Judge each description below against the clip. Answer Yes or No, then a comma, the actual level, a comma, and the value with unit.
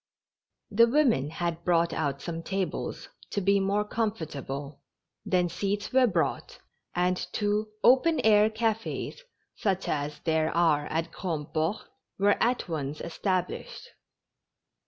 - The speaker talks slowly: Yes, slow, 120 wpm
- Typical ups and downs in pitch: Yes, average, 4.7 semitones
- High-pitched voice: No, medium, 180 Hz